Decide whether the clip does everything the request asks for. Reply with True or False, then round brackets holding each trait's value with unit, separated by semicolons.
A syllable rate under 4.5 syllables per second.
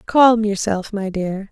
True (3.6 syllables/s)